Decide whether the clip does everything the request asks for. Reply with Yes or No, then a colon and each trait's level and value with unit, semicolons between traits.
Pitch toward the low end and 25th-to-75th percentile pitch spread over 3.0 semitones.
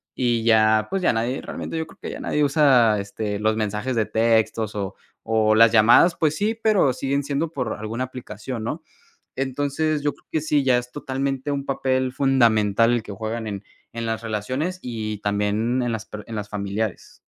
Yes: low, 115 Hz; average, 4.0 semitones